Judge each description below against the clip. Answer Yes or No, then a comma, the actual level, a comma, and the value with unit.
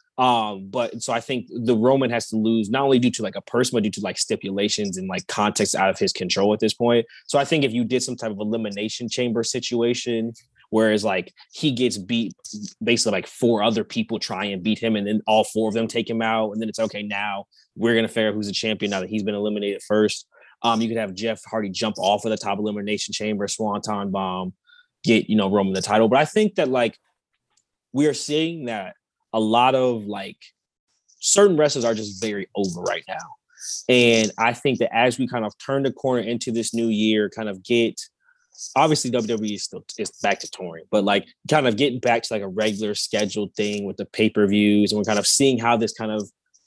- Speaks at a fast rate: Yes, fast, 230 wpm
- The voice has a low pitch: Yes, low, 110 Hz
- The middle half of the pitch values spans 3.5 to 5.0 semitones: No, average, 2.8 semitones